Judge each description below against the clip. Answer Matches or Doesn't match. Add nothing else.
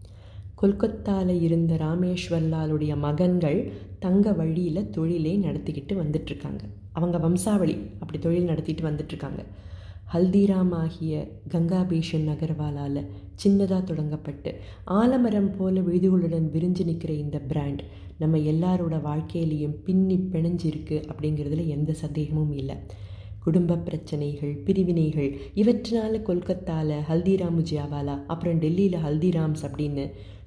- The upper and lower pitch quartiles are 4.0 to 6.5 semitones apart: Doesn't match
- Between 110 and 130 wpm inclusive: Doesn't match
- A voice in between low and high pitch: Matches